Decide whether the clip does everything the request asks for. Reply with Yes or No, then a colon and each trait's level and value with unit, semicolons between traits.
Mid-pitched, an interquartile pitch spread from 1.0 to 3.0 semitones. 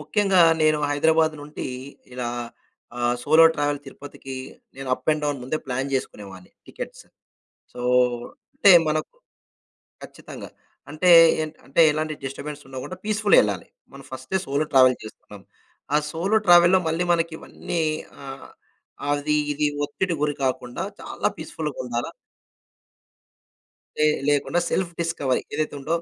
No: medium, 150 Hz; average, 3.6 semitones